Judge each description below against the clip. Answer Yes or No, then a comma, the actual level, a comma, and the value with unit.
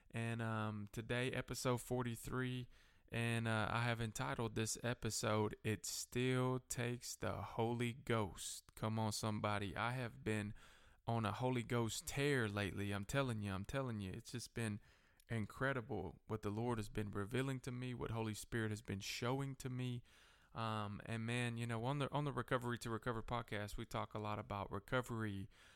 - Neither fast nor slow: Yes, average, 175 wpm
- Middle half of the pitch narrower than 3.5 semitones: Yes, average, 2.8 semitones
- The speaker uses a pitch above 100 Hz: Yes, low, 115 Hz